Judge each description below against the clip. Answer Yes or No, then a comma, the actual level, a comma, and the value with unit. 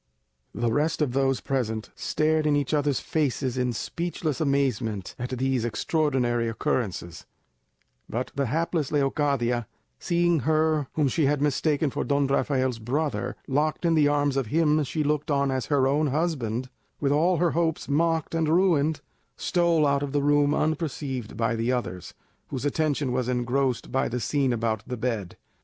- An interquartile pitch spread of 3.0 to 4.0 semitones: Yes, average, 3.7 semitones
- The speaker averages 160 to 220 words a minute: Yes, average, 165 wpm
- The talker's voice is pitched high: No, medium, 140 Hz